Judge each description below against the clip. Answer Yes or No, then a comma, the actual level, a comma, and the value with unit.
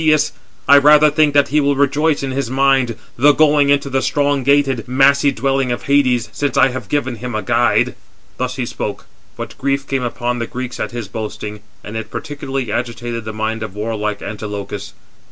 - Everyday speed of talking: No, fast, 210 wpm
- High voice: No, low, 130 Hz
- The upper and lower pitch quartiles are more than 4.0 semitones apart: No, average, 3.6 semitones